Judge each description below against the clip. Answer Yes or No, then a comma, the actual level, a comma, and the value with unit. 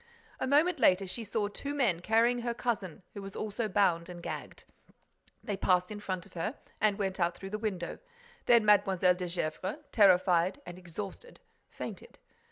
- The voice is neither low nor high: No, high, 195 Hz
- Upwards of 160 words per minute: Yes, average, 175 wpm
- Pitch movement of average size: Yes, average, 3.5 semitones